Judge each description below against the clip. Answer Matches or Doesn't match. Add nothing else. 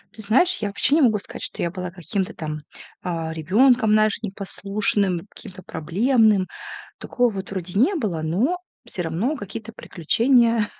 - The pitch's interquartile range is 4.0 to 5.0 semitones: Matches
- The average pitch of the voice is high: Matches